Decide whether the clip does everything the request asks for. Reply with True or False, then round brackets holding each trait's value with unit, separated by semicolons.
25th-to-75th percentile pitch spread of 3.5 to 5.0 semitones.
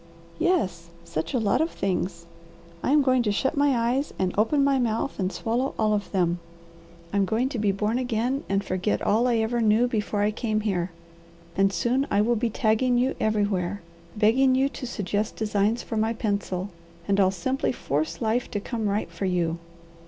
True (3.8 semitones)